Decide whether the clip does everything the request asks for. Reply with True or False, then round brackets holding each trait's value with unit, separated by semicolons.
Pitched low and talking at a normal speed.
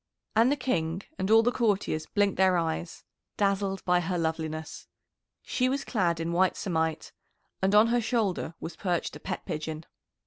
False (185 Hz; 170 wpm)